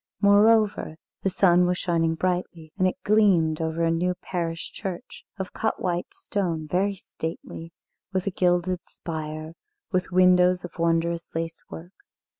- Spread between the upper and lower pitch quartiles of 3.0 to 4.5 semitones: No, narrow, 2.4 semitones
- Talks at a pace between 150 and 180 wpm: No, average, 140 wpm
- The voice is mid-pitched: Yes, medium, 180 Hz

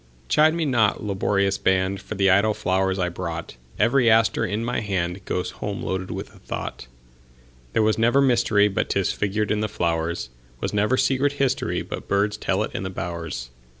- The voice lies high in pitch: No, low, 100 Hz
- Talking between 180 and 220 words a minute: No, average, 155 wpm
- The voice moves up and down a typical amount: Yes, average, 4.3 semitones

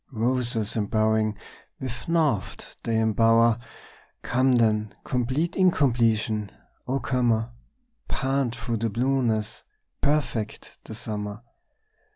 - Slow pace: Yes, slow, 95 wpm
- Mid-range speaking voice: No, low, 115 Hz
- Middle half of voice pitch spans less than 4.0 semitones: Yes, average, 2.9 semitones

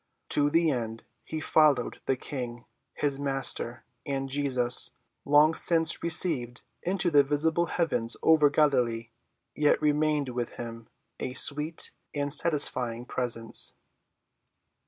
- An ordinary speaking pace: No, slow, 115 wpm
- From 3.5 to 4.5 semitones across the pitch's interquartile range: Yes, average, 3.9 semitones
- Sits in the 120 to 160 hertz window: Yes, medium, 140 Hz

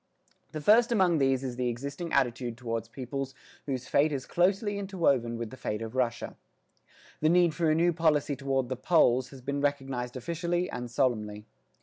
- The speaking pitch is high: No, low, 135 Hz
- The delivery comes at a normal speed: Yes, average, 180 wpm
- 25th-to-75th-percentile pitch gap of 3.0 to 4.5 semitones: No, average, 5.1 semitones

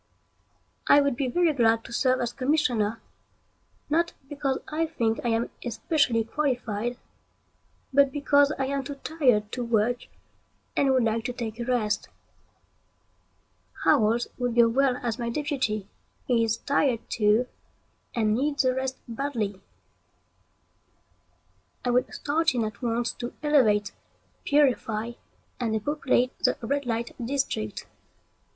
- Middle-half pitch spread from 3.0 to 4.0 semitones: Yes, average, 3.6 semitones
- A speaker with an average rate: No, slow, 130 wpm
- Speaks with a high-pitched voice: Yes, high, 245 Hz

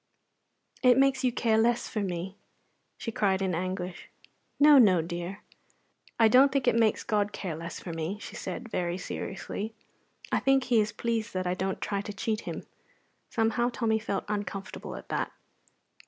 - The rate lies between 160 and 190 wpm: Yes, average, 170 wpm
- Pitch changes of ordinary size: Yes, average, 3.9 semitones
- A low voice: No, high, 210 Hz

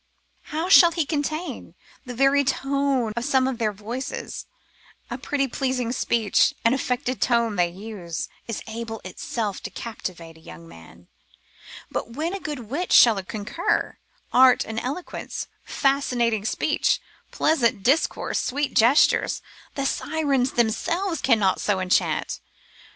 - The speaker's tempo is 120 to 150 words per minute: Yes, slow, 135 wpm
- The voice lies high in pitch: Yes, high, 245 Hz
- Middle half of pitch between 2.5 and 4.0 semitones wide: No, average, 4.5 semitones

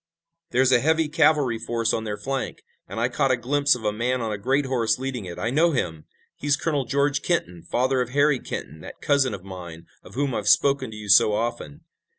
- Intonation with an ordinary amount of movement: Yes, average, 4.5 semitones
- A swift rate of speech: Yes, fast, 220 wpm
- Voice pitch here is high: No, low, 125 Hz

